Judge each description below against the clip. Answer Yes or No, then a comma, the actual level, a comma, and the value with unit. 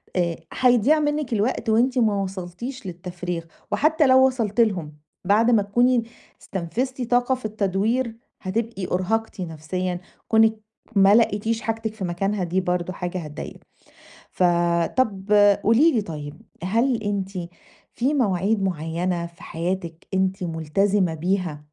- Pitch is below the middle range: No, high, 200 Hz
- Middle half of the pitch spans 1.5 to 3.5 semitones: No, average, 4.4 semitones